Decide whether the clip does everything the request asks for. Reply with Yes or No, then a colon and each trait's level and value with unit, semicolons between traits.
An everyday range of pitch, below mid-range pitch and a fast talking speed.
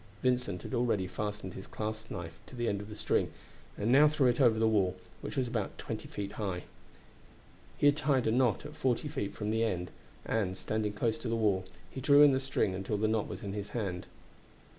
Yes: average, 3.8 semitones; low, 110 Hz; fast, 225 wpm